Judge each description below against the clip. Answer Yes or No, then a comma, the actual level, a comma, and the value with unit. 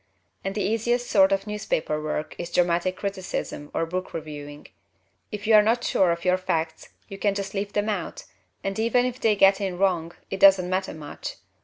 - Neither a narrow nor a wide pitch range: Yes, average, 3.3 semitones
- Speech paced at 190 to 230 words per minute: Yes, average, 195 wpm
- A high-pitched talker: Yes, high, 195 Hz